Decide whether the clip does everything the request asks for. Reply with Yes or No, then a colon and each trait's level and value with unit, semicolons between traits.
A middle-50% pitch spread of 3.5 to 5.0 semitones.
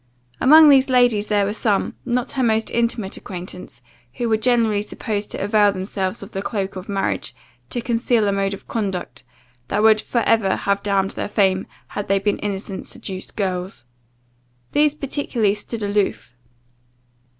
No: average, 3.0 semitones